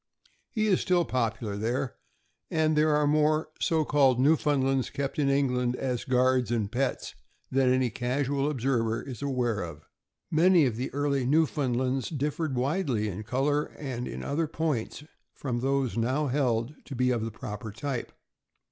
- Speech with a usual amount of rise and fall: Yes, average, 3.3 semitones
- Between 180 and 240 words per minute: No, average, 155 wpm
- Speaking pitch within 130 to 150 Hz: Yes, low, 135 Hz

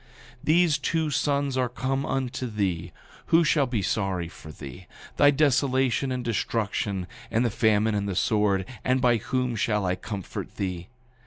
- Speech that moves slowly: No, average, 155 wpm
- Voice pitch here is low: Yes, low, 120 Hz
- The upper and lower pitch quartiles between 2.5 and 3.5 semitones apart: No, average, 5.1 semitones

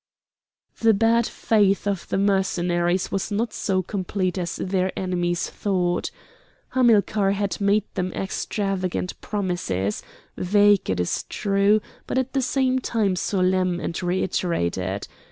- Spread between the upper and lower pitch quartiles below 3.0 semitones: Yes, narrow, 2.5 semitones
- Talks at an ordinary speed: No, slow, 125 wpm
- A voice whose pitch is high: Yes, high, 195 Hz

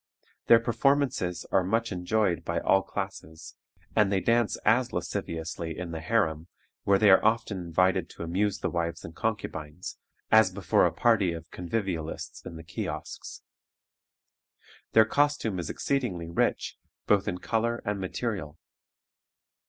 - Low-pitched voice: Yes, very low, 95 Hz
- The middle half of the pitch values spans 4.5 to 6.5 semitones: Yes, average, 4.9 semitones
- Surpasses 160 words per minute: No, average, 140 wpm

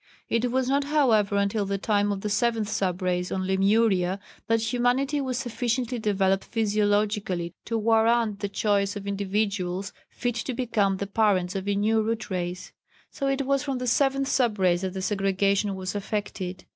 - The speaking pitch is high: Yes, high, 205 Hz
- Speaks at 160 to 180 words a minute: Yes, average, 175 wpm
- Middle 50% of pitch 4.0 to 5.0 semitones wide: No, average, 3.4 semitones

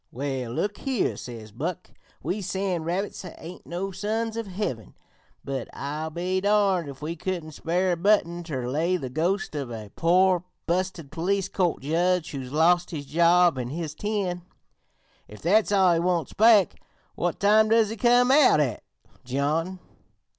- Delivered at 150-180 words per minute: Yes, average, 160 wpm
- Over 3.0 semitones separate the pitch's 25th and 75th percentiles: Yes, average, 4.4 semitones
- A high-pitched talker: No, medium, 175 Hz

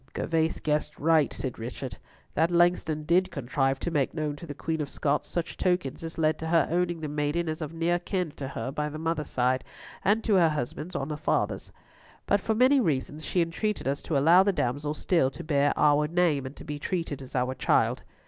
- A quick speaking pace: Yes, fast, 215 wpm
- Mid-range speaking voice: Yes, medium, 155 Hz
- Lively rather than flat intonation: No, average, 3.1 semitones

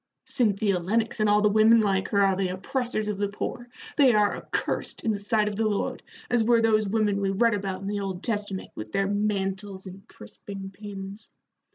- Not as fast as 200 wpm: No, fast, 205 wpm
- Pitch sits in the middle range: No, high, 205 Hz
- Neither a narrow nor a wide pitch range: No, narrow, 1.8 semitones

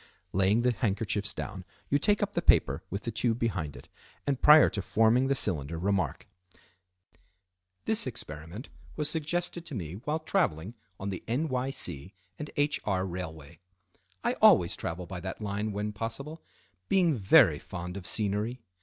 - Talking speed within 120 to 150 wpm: No, average, 160 wpm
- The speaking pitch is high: No, low, 105 Hz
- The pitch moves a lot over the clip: Yes, wide, 6.6 semitones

